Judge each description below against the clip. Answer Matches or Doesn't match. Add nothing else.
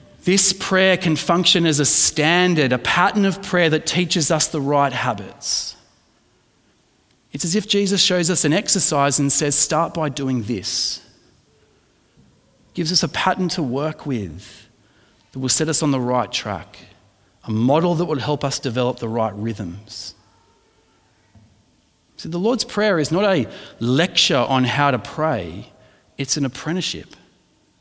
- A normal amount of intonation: Doesn't match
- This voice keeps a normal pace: Matches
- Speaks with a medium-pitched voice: Matches